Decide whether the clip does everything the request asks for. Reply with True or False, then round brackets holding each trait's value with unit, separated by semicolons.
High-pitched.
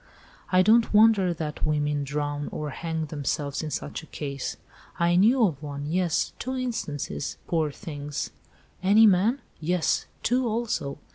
False (165 Hz)